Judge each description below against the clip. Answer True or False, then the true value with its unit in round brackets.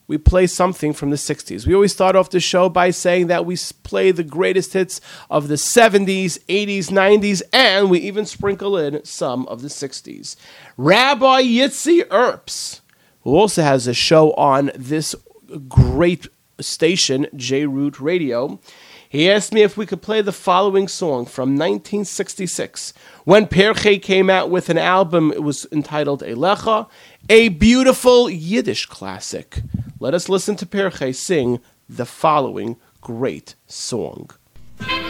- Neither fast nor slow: True (145 wpm)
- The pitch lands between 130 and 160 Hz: False (180 Hz)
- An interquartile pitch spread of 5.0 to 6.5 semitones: True (5.3 semitones)